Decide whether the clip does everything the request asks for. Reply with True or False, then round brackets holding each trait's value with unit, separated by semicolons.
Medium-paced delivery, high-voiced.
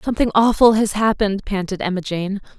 True (165 wpm; 205 Hz)